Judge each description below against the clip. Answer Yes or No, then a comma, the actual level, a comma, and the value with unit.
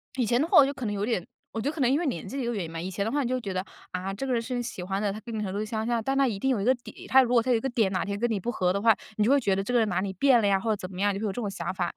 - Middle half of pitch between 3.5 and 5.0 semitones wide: Yes, average, 4.0 semitones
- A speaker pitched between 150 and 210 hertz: No, high, 220 Hz